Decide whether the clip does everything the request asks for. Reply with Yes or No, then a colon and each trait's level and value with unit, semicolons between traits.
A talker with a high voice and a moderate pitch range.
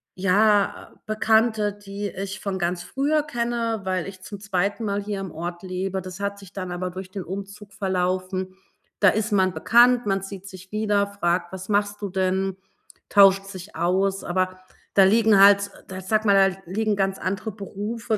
No: high, 195 Hz; narrow, 1.9 semitones